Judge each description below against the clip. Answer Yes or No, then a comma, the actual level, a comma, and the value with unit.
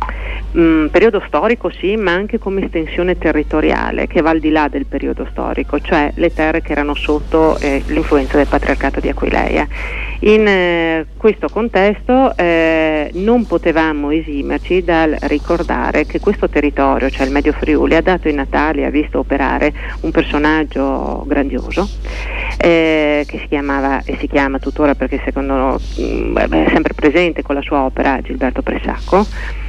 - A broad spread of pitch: No, average, 3.3 semitones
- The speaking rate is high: No, average, 155 wpm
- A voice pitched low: No, medium, 155 Hz